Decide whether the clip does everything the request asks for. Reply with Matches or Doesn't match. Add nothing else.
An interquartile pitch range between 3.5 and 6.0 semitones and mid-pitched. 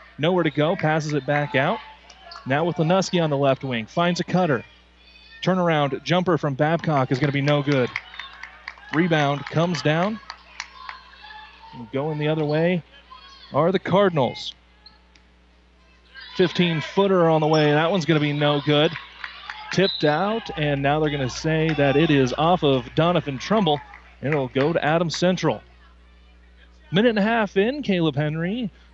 Matches